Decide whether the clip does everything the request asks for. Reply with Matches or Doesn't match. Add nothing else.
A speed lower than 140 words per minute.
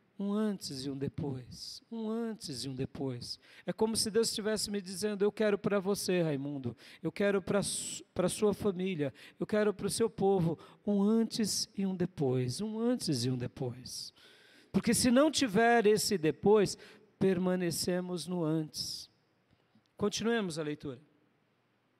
Doesn't match